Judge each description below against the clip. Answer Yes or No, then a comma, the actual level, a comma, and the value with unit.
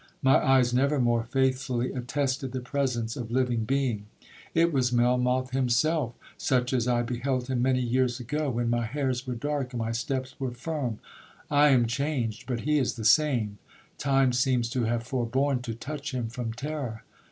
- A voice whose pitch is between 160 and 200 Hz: No, low, 125 Hz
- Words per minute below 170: No, average, 175 wpm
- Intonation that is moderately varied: No, narrow, 2.2 semitones